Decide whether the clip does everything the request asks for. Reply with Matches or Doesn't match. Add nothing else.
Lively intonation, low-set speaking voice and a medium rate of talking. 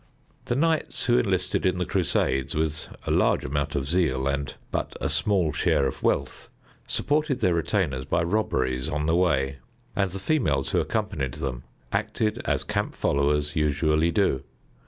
Matches